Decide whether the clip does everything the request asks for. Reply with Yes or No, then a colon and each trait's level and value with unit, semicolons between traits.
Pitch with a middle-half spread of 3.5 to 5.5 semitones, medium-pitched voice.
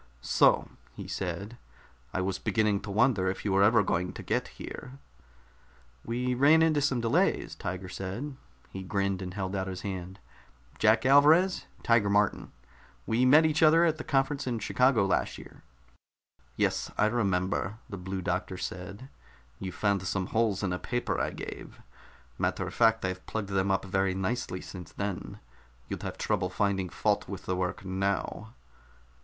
No: average, 4.4 semitones; low, 100 Hz